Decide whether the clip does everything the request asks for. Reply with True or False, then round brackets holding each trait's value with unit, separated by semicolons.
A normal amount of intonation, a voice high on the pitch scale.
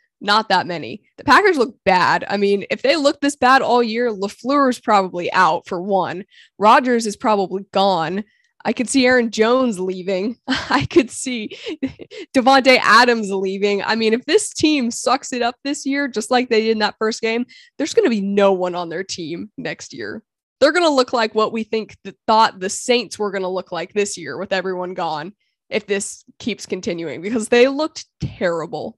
True (4.8 semitones; 225 Hz)